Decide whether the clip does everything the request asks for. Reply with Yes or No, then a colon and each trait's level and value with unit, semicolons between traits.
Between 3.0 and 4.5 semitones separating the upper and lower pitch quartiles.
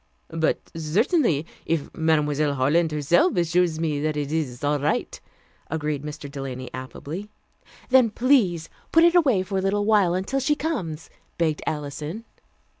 No: average, 5.2 semitones